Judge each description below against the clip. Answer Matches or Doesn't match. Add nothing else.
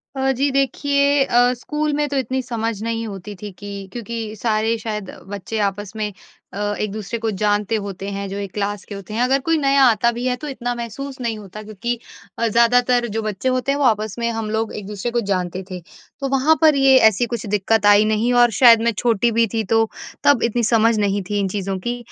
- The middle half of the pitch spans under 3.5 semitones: Matches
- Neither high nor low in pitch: Doesn't match